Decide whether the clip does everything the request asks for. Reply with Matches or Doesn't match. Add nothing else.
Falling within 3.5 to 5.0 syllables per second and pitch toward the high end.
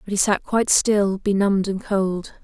Matches